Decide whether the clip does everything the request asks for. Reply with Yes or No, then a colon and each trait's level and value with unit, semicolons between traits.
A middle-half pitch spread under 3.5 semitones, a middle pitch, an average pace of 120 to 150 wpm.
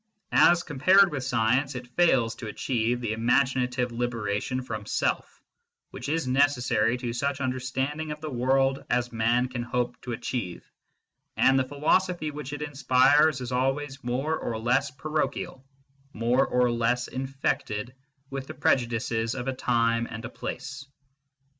No: narrow, 2.6 semitones; low, 130 Hz; average, 145 wpm